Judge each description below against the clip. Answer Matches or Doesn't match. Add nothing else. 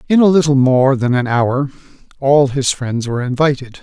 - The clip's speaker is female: Doesn't match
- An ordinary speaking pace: Matches